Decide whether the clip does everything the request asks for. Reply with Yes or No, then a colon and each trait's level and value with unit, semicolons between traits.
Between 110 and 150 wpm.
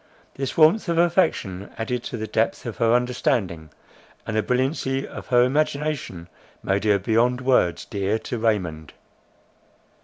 Yes: average, 145 wpm